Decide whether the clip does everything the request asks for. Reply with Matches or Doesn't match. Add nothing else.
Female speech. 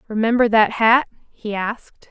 Matches